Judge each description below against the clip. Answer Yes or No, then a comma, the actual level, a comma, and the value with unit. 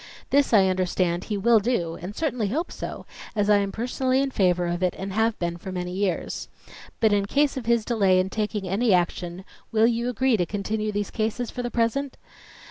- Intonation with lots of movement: No, average, 4.1 semitones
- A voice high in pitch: Yes, high, 210 Hz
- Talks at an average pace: No, fast, 210 wpm